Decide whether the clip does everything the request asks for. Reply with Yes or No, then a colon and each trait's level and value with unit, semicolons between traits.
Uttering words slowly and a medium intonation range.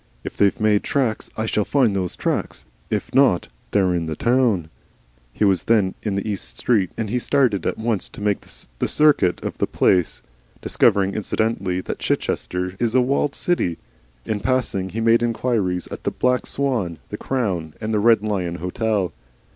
No: average, 175 wpm; average, 4.3 semitones